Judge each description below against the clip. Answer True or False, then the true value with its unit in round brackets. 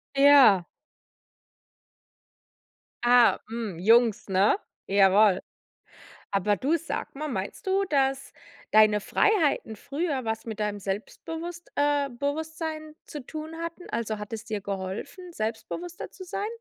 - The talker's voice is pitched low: False (255 Hz)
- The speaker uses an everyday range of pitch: False (7.0 semitones)